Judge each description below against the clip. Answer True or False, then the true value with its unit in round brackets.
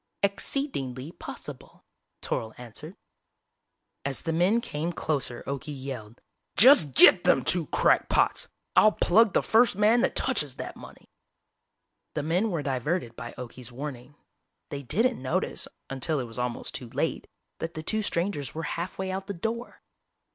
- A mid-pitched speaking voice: True (155 Hz)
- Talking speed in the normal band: True (155 wpm)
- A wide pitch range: True (7.2 semitones)